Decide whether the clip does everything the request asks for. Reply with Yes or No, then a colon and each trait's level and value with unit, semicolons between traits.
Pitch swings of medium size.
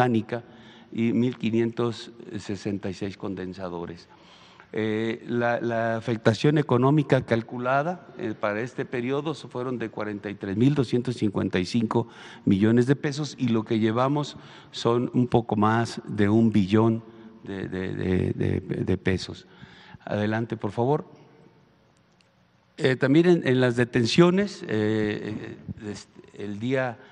Yes: average, 3.3 semitones